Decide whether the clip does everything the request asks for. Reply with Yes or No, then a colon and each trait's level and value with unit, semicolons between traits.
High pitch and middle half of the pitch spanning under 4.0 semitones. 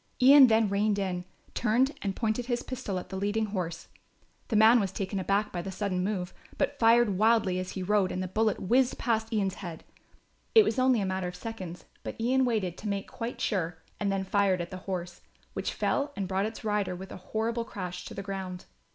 Yes: high, 200 Hz; average, 3.3 semitones